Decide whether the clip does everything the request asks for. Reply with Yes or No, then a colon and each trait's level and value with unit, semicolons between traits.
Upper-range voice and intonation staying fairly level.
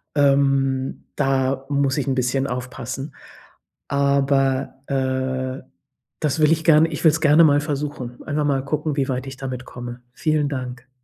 No: low, 135 Hz; narrow, 1.8 semitones